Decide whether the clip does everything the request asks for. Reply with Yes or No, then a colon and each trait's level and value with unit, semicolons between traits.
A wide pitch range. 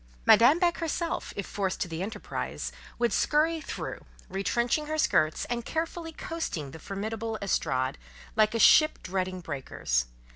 Yes: wide, 9.0 semitones